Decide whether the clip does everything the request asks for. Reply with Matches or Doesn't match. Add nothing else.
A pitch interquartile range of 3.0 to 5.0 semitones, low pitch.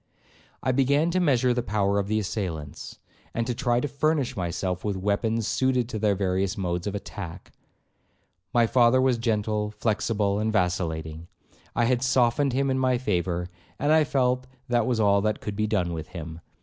Matches